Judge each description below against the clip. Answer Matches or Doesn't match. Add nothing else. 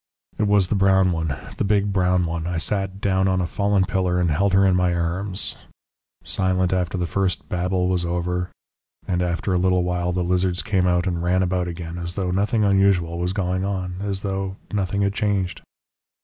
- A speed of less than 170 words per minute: Doesn't match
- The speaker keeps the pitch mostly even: Matches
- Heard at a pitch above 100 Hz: Doesn't match